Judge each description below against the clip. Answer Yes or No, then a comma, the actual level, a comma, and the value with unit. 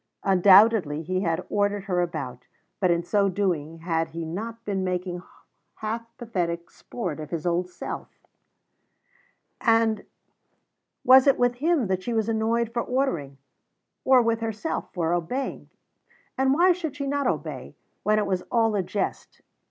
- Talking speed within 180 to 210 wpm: No, average, 150 wpm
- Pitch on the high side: Yes, high, 205 Hz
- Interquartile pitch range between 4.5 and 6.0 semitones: Yes, average, 4.9 semitones